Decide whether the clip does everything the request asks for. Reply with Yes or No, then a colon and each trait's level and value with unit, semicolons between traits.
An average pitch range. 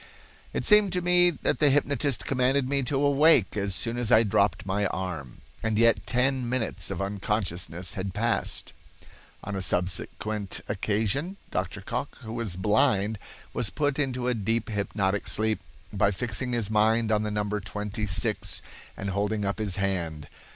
Yes: average, 4.1 semitones